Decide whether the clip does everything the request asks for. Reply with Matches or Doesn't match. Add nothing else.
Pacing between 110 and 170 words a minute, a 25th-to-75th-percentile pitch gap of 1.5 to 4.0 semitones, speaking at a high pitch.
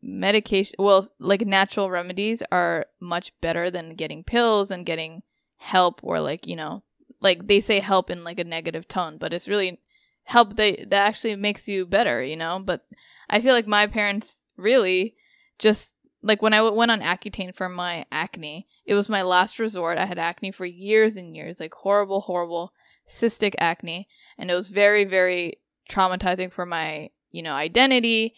Doesn't match